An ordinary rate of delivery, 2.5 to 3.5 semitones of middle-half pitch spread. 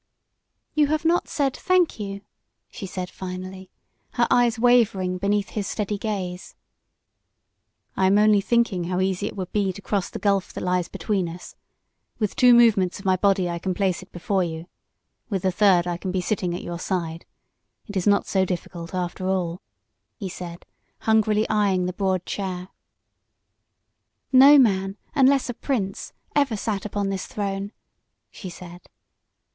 Yes: average, 165 wpm; average, 2.8 semitones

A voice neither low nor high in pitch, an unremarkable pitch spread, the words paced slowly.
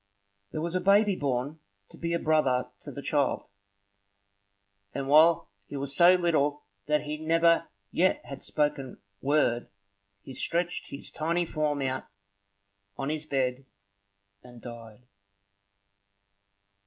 Yes: medium, 150 Hz; average, 3.7 semitones; slow, 130 wpm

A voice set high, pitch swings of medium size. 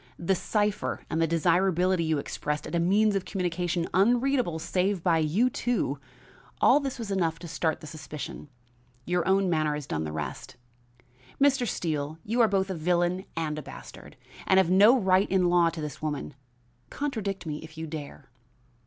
No: medium, 175 Hz; average, 3.6 semitones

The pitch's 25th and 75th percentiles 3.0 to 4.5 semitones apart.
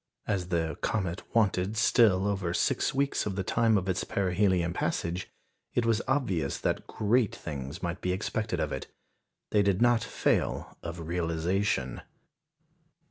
Yes: average, 3.9 semitones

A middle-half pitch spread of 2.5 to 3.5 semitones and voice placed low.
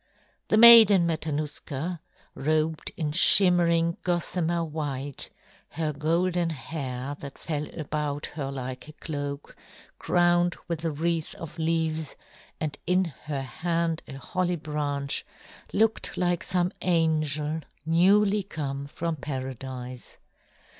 No: average, 3.1 semitones; medium, 160 Hz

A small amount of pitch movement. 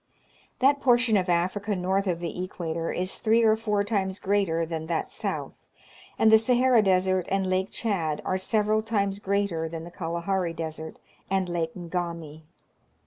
No: average, 3.5 semitones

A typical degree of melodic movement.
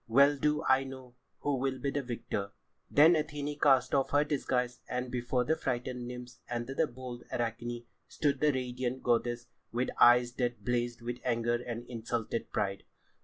No: narrow, 2.2 semitones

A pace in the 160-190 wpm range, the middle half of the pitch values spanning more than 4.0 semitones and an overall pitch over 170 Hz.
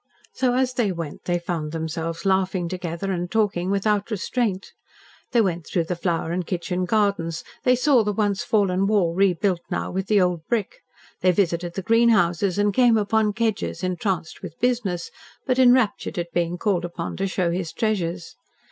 No: average, 175 wpm; average, 3.7 semitones; high, 190 Hz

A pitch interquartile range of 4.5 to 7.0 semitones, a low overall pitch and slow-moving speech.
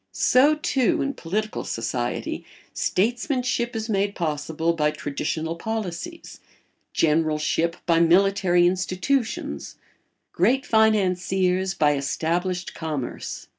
No: average, 5.1 semitones; medium, 185 Hz; slow, 95 wpm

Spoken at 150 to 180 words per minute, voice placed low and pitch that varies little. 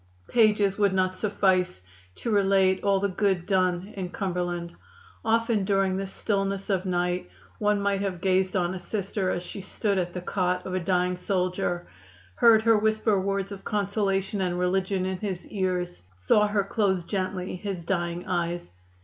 No: average, 165 wpm; high, 190 Hz; narrow, 1.8 semitones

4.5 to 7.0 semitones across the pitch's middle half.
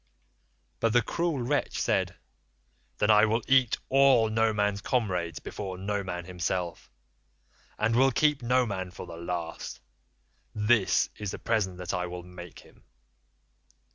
Yes: average, 4.8 semitones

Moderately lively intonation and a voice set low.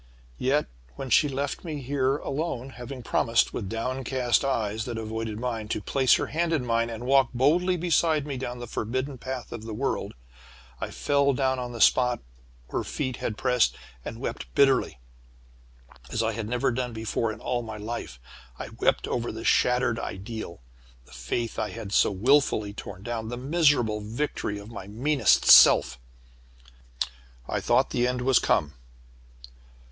Yes: average, 3.3 semitones; low, 120 Hz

